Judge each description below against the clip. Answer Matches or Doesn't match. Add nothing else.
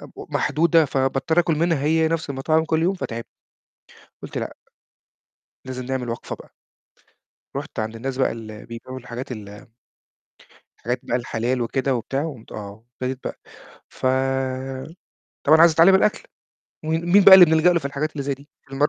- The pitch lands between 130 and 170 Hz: Matches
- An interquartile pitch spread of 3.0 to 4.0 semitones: Doesn't match